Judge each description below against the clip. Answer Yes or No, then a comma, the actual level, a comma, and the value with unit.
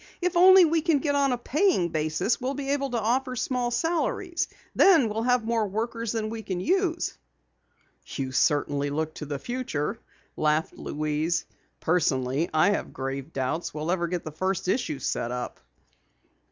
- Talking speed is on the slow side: No, average, 165 wpm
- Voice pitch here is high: Yes, high, 215 Hz